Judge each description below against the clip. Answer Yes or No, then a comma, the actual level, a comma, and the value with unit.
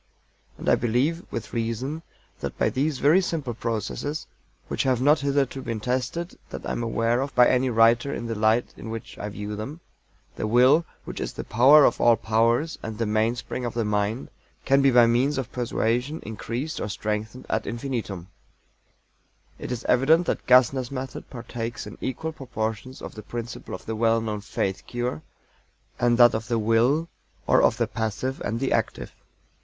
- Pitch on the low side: Yes, low, 120 Hz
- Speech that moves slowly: No, average, 180 wpm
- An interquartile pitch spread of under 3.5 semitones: Yes, average, 3.0 semitones